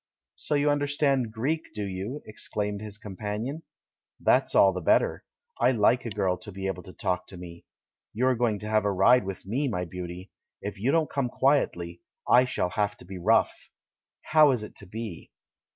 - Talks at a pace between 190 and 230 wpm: Yes, average, 200 wpm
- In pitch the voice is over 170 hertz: No, low, 105 Hz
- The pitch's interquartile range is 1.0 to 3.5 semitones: No, average, 5.1 semitones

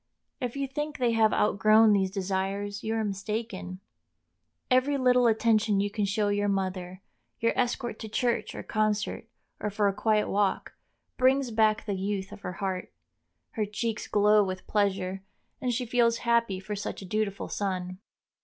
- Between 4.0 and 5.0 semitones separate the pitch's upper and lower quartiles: No, average, 2.8 semitones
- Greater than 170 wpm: No, average, 160 wpm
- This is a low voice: No, high, 210 Hz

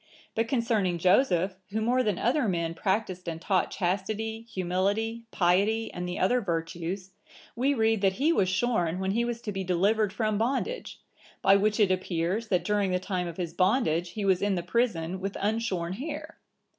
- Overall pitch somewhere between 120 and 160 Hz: No, high, 195 Hz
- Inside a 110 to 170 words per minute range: No, average, 180 wpm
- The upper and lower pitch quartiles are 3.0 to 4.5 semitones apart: Yes, average, 3.7 semitones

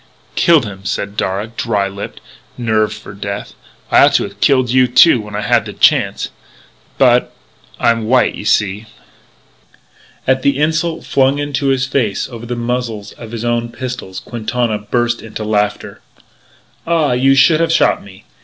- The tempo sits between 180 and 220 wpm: No, average, 165 wpm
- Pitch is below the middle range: Yes, low, 120 Hz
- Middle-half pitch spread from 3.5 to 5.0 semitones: Yes, average, 3.9 semitones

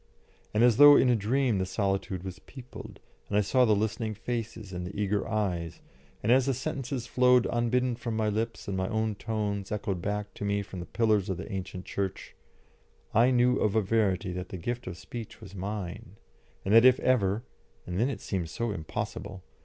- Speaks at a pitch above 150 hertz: No, low, 105 Hz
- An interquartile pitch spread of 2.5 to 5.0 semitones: Yes, average, 3.6 semitones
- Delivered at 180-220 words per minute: Yes, average, 200 wpm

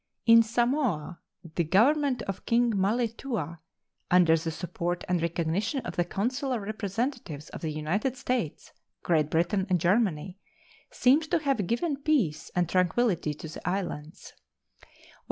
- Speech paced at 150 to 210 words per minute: No, slow, 135 wpm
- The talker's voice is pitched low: No, high, 195 Hz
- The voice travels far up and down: Yes, wide, 6.3 semitones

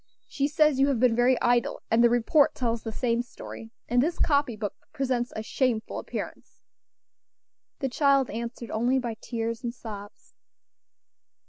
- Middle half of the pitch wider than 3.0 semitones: No, average, 2.7 semitones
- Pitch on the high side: Yes, high, 240 Hz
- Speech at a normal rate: Yes, average, 155 wpm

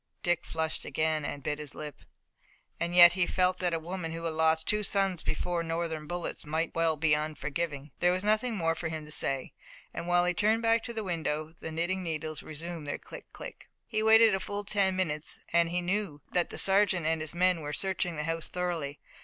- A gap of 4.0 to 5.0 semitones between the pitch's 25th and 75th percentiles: No, average, 2.8 semitones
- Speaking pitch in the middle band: Yes, medium, 170 Hz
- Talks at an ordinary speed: No, fast, 215 wpm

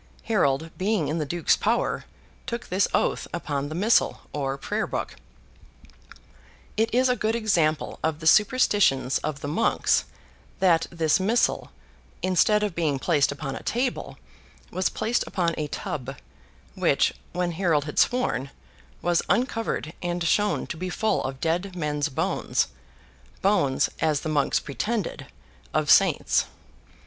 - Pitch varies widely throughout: Yes, wide, 5.9 semitones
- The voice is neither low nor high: Yes, medium, 170 Hz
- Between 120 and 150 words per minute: Yes, average, 140 wpm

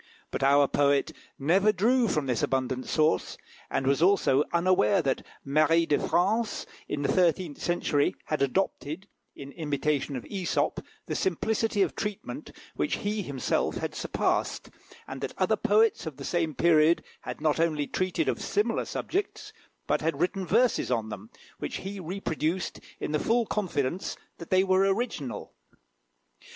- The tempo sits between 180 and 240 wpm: No, average, 155 wpm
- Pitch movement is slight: No, wide, 5.4 semitones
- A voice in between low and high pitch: Yes, medium, 165 Hz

